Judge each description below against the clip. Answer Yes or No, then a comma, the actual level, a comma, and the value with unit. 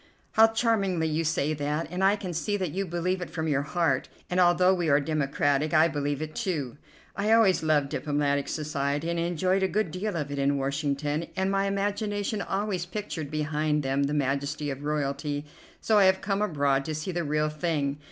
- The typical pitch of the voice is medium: Yes, medium, 155 Hz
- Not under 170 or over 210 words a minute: Yes, average, 200 wpm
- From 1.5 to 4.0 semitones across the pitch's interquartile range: No, average, 4.6 semitones